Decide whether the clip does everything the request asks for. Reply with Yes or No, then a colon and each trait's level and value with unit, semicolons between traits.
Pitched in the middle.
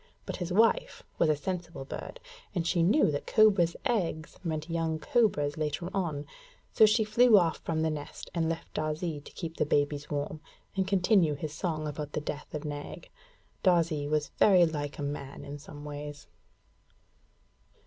Yes: medium, 160 Hz